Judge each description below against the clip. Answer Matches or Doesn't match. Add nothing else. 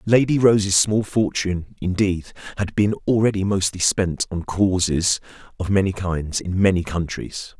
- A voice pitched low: Matches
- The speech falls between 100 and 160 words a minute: Matches